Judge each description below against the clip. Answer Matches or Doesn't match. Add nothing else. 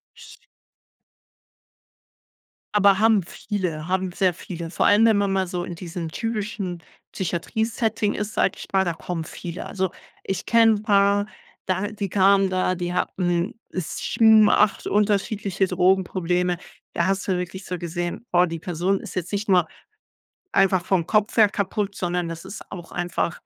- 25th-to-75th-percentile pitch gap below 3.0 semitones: Matches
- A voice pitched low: Doesn't match